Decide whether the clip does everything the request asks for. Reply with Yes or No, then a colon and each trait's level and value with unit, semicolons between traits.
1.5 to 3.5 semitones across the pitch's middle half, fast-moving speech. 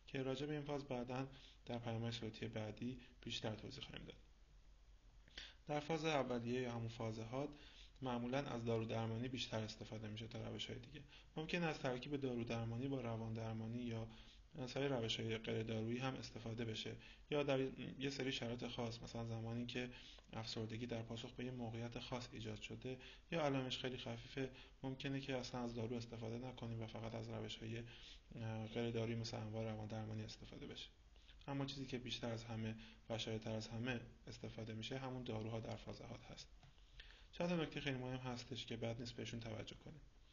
Yes: narrow, 2.5 semitones; fast, 175 wpm